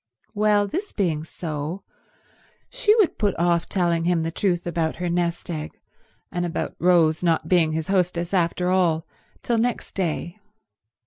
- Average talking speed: Yes, average, 150 wpm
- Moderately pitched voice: Yes, medium, 175 Hz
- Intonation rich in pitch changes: No, average, 2.7 semitones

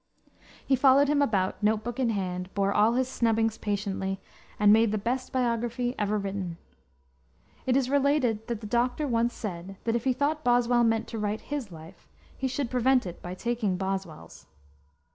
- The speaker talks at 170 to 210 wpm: Yes, average, 180 wpm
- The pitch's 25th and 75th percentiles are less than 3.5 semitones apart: No, average, 3.9 semitones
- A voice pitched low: No, high, 225 Hz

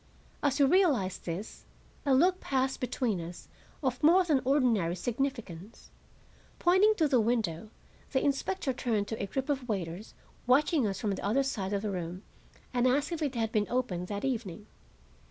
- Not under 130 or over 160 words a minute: No, average, 175 wpm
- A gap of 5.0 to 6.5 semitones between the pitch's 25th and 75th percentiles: Yes, wide, 5.5 semitones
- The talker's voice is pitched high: Yes, high, 245 Hz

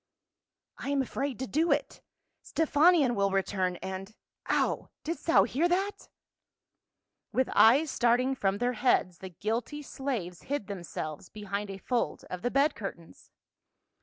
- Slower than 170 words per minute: Yes, average, 155 wpm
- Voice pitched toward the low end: No, high, 240 Hz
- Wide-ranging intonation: Yes, wide, 6.4 semitones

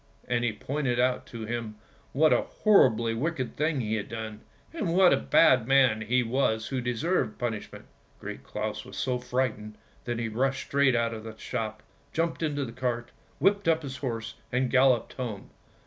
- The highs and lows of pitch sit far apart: No, average, 3.4 semitones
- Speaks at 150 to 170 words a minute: No, average, 185 wpm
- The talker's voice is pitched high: No, low, 125 Hz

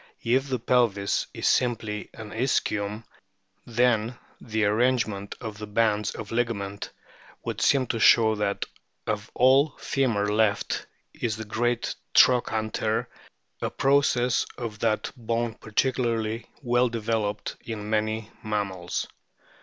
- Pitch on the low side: Yes, low, 110 Hz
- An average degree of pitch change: No, narrow, 2.3 semitones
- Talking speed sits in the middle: No, slow, 120 wpm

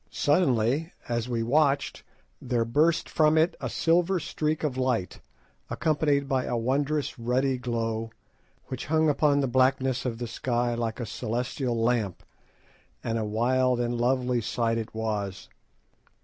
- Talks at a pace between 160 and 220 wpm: No, average, 145 wpm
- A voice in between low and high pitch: No, low, 125 Hz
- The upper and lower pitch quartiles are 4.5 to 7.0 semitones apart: No, average, 3.6 semitones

